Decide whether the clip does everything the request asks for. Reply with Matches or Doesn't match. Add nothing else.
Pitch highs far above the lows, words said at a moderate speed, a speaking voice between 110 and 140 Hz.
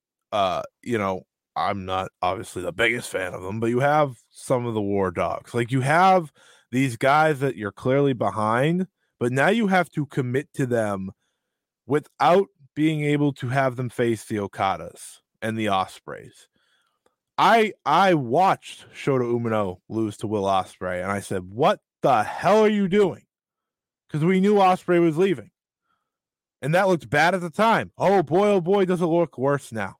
Matches